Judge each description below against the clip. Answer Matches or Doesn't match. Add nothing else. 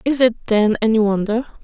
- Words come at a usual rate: Matches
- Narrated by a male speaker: Doesn't match